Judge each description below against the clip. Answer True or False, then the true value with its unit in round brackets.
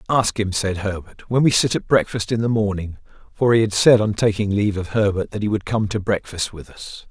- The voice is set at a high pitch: False (105 Hz)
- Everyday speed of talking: False (245 wpm)